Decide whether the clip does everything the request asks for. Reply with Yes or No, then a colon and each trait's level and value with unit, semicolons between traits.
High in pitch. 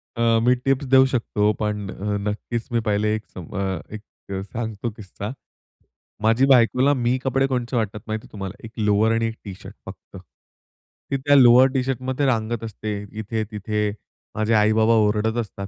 No: low, 115 Hz